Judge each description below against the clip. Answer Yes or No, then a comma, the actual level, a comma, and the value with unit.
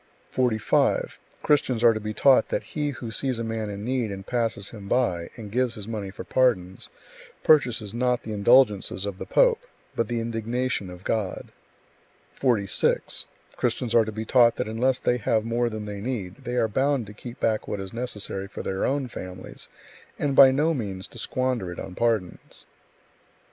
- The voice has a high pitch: No, low, 115 Hz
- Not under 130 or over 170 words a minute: No, average, 185 wpm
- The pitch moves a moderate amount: Yes, average, 3.6 semitones